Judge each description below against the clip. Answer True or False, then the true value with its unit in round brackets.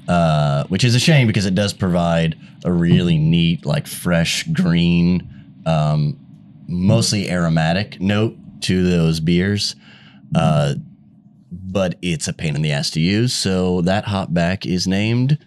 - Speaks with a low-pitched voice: True (95 Hz)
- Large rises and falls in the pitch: True (6.7 semitones)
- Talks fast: False (145 wpm)